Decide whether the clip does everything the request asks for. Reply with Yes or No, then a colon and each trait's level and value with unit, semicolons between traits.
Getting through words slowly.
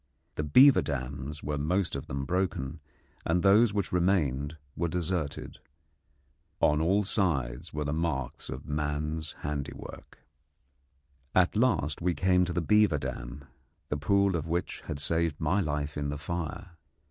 No: average, 145 wpm